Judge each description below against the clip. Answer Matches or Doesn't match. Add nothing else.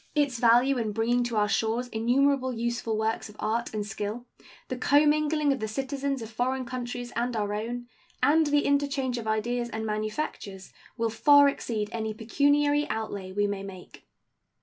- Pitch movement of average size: Matches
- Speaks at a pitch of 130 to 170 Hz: Doesn't match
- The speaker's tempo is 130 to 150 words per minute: Doesn't match